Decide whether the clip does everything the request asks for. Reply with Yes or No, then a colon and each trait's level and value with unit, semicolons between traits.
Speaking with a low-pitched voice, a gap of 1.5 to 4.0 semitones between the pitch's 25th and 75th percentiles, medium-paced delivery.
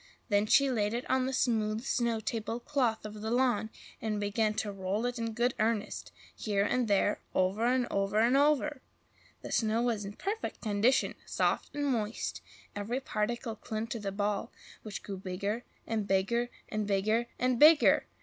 No: high, 220 Hz; average, 2.8 semitones; average, 175 wpm